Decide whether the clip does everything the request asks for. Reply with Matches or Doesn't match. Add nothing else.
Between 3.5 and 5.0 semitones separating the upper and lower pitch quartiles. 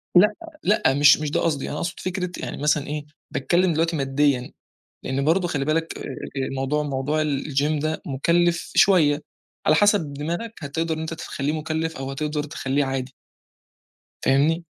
Doesn't match